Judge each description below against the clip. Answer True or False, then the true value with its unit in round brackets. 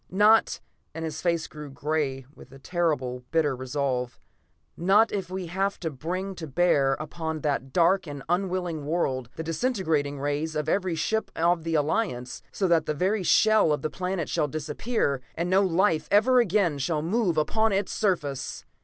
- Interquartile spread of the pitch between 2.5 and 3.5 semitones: False (4.4 semitones)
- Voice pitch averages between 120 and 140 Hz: False (165 Hz)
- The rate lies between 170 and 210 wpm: True (175 wpm)